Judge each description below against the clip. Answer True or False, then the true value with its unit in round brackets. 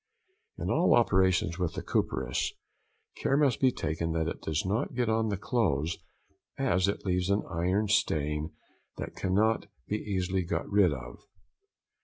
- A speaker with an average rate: True (155 wpm)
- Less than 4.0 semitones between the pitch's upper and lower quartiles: False (4.3 semitones)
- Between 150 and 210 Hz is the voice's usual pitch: False (95 Hz)